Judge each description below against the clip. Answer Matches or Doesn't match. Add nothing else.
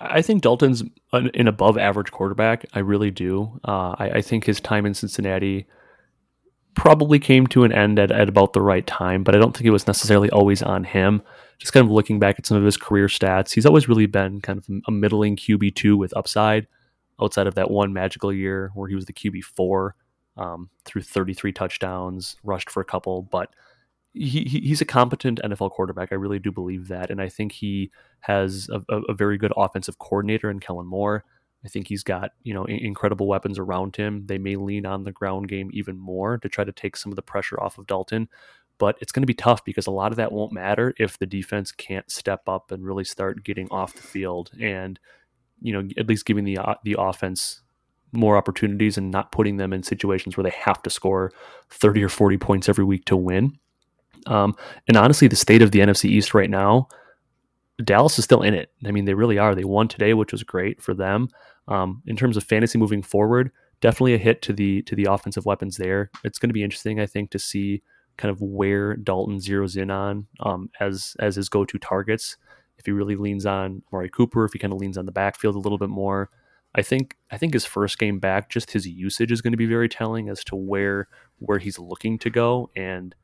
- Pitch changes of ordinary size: Doesn't match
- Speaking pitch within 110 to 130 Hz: Doesn't match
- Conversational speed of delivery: Doesn't match